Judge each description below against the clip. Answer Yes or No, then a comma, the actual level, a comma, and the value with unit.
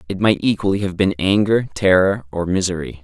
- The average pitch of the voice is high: No, very low, 95 Hz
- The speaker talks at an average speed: Yes, average, 180 wpm